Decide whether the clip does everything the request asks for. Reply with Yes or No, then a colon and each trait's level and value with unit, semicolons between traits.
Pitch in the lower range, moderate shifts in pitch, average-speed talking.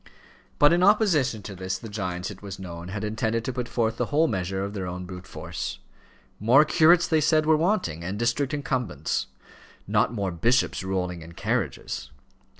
No: low, 110 Hz; wide, 7.9 semitones; average, 175 wpm